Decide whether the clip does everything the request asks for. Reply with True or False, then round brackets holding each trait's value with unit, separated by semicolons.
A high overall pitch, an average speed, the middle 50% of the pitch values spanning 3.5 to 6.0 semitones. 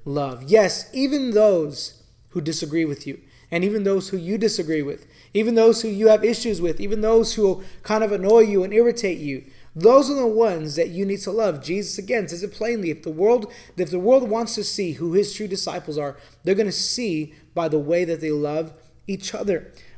False (195 Hz; 220 wpm; 5.3 semitones)